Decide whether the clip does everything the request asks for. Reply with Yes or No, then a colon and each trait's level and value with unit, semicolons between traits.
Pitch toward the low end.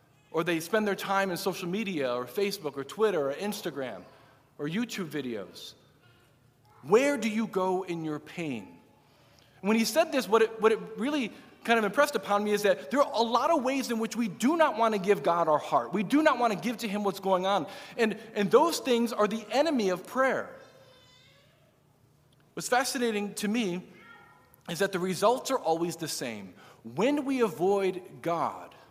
No: high, 195 Hz